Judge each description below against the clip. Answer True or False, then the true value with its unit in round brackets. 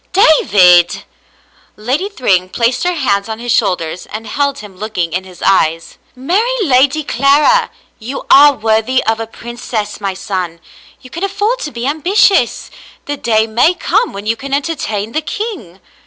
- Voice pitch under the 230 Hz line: False (240 Hz)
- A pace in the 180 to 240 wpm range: False (170 wpm)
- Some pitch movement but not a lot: False (6.5 semitones)